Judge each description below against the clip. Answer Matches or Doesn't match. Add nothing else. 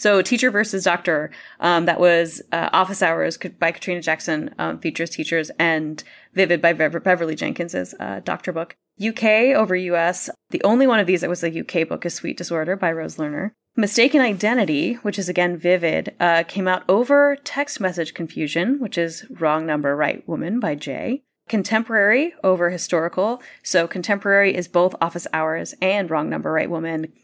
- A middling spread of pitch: Matches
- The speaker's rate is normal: Matches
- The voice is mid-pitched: Matches